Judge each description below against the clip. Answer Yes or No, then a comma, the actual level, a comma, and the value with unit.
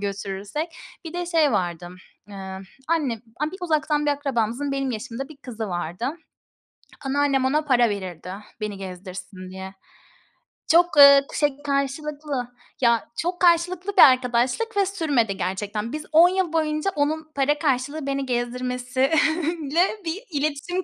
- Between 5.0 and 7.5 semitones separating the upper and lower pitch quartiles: Yes, wide, 5.5 semitones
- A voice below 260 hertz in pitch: No, very high, 275 Hz